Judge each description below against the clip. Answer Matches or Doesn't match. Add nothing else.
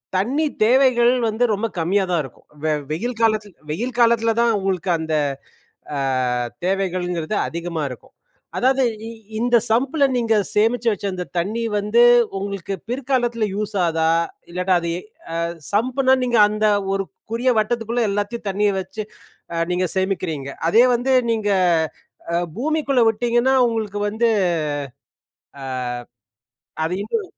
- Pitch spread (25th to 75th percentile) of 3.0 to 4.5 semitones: Matches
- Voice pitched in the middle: Doesn't match